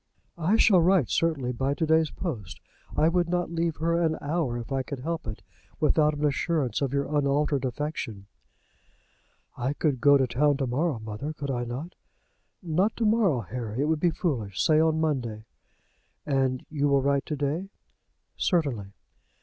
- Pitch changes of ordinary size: Yes, average, 4.1 semitones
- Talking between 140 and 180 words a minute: Yes, average, 175 wpm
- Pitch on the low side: No, medium, 145 Hz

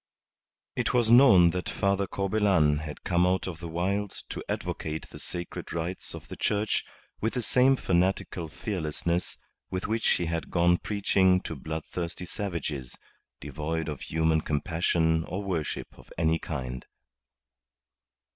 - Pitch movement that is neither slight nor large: Yes, average, 3.4 semitones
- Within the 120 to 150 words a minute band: Yes, average, 140 wpm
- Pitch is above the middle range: No, very low, 85 Hz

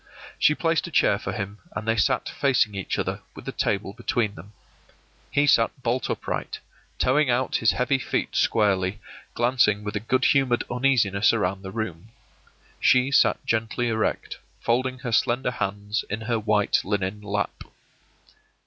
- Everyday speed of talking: Yes, average, 160 wpm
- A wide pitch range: No, average, 3.4 semitones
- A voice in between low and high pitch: No, low, 110 Hz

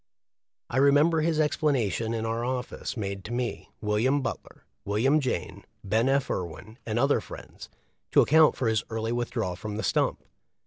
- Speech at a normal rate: Yes, average, 165 wpm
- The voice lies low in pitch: Yes, low, 120 Hz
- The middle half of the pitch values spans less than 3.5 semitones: No, average, 4.2 semitones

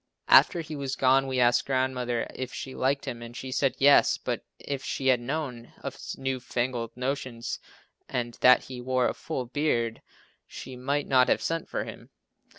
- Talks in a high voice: No, low, 130 Hz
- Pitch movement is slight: Yes, narrow, 1.8 semitones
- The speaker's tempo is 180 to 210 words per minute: Yes, average, 185 wpm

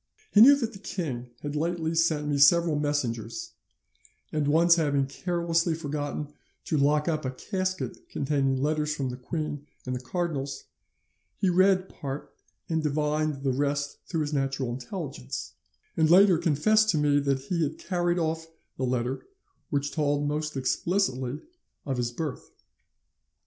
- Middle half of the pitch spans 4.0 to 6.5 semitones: No, average, 3.4 semitones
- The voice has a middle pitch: Yes, medium, 150 Hz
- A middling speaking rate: Yes, average, 150 wpm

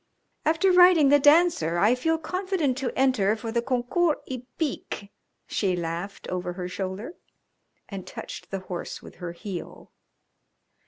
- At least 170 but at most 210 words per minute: No, average, 140 wpm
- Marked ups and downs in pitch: Yes, wide, 8.8 semitones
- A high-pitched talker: Yes, high, 245 Hz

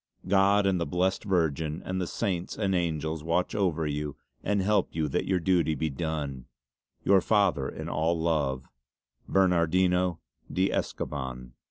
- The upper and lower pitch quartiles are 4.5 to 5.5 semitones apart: No, average, 3.4 semitones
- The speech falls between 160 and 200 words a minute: No, average, 150 wpm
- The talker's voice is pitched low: Yes, very low, 85 Hz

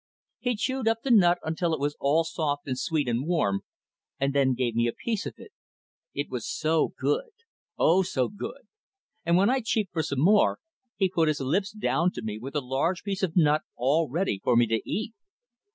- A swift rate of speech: Yes, fast, 210 wpm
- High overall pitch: No, medium, 160 Hz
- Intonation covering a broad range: Yes, wide, 6.2 semitones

